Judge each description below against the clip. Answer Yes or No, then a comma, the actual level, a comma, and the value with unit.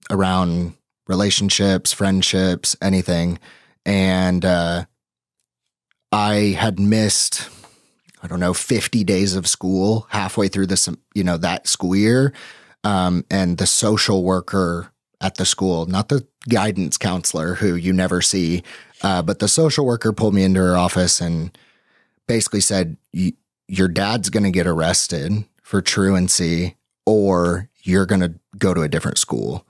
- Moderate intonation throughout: No, narrow, 2.3 semitones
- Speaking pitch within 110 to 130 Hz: No, very low, 95 Hz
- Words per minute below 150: Yes, slow, 135 wpm